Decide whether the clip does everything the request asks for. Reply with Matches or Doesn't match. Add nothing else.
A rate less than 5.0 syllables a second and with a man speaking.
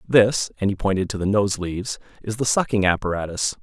Doesn't match